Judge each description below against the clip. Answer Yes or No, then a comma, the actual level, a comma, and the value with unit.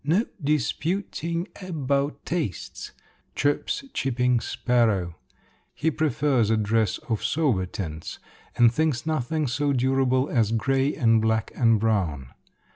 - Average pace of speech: No, slow, 130 wpm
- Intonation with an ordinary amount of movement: Yes, average, 4.8 semitones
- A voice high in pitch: No, low, 125 Hz